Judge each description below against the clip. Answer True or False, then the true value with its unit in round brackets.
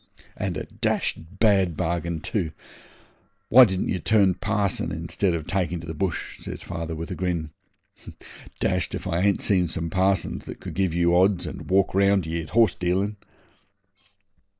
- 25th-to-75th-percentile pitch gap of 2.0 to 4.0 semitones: True (2.8 semitones)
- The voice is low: True (90 Hz)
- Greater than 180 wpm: False (170 wpm)